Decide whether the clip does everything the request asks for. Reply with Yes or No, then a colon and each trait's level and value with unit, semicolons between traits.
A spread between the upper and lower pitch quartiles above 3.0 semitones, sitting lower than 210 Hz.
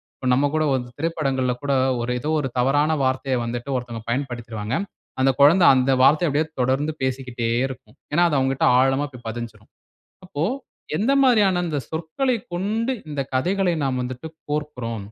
Yes: average, 4.0 semitones; low, 135 Hz